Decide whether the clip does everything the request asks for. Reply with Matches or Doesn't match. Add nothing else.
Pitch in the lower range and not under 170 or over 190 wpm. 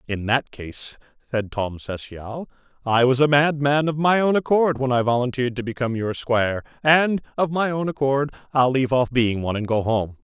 Doesn't match